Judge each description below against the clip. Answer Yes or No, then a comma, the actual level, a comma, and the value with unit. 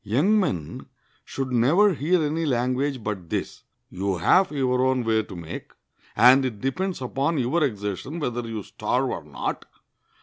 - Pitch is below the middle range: Yes, low, 130 Hz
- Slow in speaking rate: No, average, 160 wpm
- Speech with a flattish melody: No, average, 5.2 semitones